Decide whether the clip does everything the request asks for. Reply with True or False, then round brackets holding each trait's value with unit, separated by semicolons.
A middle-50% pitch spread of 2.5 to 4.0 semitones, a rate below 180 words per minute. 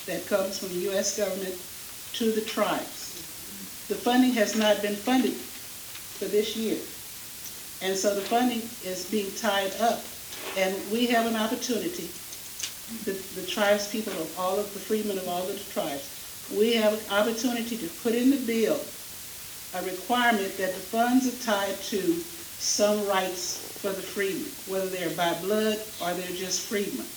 True (2.9 semitones; 165 wpm)